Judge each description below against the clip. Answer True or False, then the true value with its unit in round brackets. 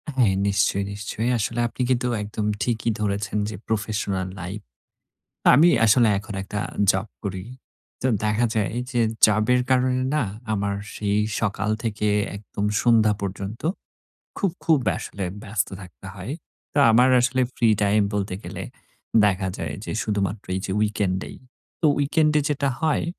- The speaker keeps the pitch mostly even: False (3.3 semitones)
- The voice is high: False (105 Hz)